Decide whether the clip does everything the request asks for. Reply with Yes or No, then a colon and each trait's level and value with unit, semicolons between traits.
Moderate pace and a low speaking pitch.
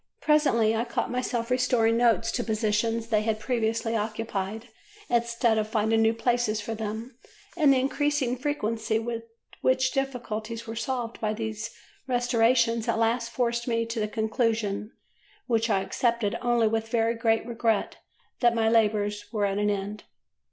No: average, 155 wpm; high, 230 Hz